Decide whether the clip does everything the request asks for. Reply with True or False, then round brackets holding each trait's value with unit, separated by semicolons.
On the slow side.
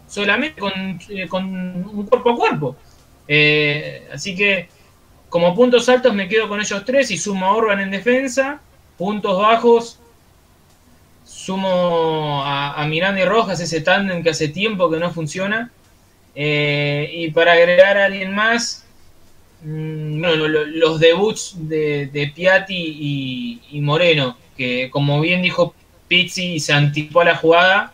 False (150 wpm)